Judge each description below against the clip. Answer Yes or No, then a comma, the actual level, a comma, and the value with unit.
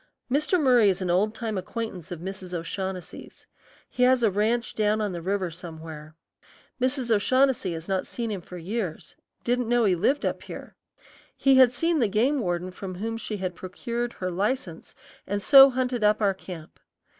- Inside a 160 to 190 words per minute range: Yes, average, 180 wpm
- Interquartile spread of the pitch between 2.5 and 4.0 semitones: No, average, 4.9 semitones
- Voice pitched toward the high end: Yes, high, 210 Hz